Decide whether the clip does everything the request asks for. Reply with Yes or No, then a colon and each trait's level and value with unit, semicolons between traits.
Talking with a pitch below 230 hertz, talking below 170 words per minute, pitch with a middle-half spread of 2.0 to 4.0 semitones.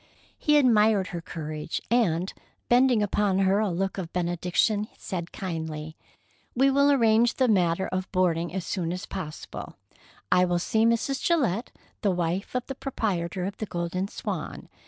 No: high, 190 Hz; average, 155 wpm; average, 4.6 semitones